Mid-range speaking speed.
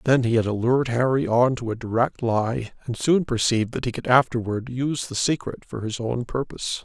No: fast, 210 wpm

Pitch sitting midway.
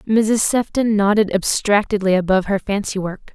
No: high, 205 Hz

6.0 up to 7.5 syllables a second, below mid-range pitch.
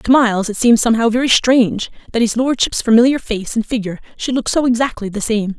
No: 6.4 syllables/s; high, 230 Hz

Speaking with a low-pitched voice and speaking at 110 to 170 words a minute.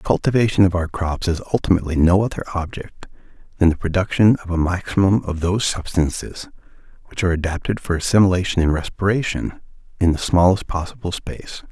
Yes: very low, 90 Hz; average, 160 wpm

